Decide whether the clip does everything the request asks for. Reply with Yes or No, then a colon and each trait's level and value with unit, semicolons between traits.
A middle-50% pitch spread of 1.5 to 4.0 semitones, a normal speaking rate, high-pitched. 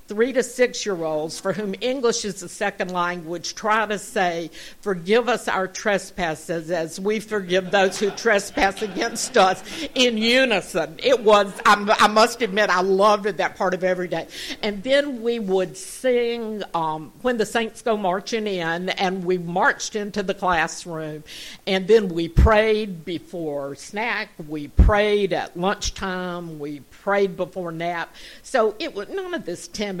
Yes: average, 3.7 semitones; average, 165 wpm; high, 200 Hz